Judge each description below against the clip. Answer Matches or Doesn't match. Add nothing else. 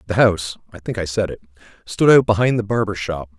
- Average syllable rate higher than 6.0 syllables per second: Matches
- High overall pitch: Doesn't match